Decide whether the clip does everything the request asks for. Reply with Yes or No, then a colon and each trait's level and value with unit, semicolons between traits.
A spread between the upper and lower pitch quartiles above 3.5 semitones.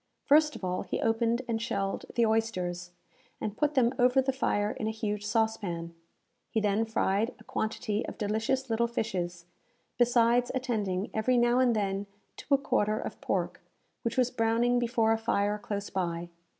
No: average, 2.9 semitones